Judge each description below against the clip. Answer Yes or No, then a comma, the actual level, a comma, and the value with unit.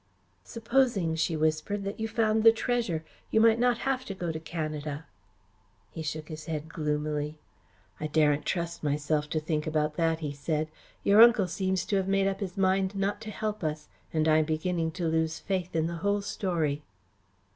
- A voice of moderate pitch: Yes, medium, 165 Hz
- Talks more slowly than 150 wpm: No, average, 185 wpm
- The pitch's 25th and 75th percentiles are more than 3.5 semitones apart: Yes, average, 4.4 semitones